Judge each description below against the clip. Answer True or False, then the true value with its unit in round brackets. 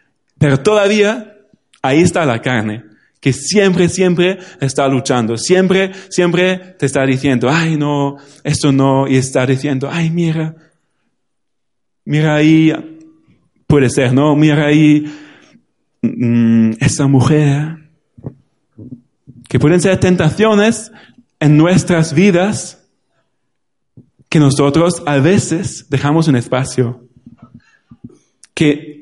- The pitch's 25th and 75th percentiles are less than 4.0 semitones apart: False (4.6 semitones)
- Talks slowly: True (105 wpm)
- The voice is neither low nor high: True (150 Hz)